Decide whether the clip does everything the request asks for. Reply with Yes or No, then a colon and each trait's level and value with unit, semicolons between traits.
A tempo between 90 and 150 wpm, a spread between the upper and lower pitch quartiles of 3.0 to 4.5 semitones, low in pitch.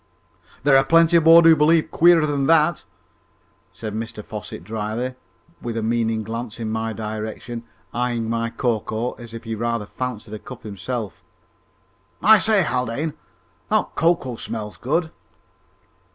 No: average, 145 wpm; average, 5.3 semitones; low, 120 Hz